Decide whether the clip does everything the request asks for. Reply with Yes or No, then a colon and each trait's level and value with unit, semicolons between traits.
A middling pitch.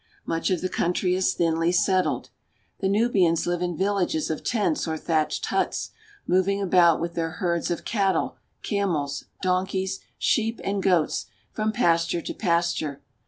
Yes: medium, 180 Hz